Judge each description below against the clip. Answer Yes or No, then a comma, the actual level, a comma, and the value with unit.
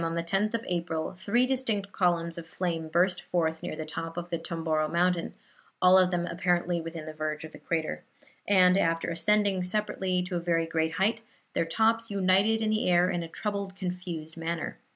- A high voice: No, medium, 175 Hz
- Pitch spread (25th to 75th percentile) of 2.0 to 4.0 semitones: Yes, average, 2.8 semitones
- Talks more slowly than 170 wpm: No, average, 195 wpm